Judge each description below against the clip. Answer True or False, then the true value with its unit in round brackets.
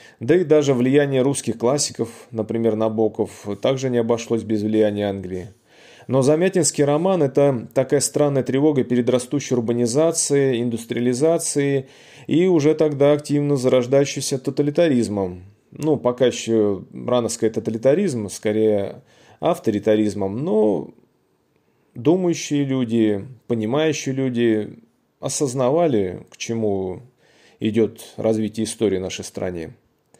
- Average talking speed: False (105 wpm)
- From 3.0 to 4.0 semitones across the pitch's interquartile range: False (4.6 semitones)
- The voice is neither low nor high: False (120 Hz)